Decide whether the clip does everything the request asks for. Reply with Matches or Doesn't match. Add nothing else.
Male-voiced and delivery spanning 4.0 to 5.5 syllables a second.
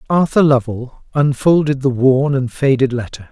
Matches